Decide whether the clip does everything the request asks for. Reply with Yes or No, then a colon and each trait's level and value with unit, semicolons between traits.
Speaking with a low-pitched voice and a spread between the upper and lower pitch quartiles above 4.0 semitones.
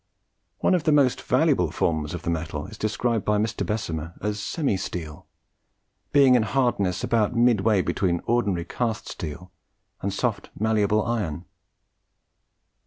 Yes: low, 105 Hz; average, 5.3 semitones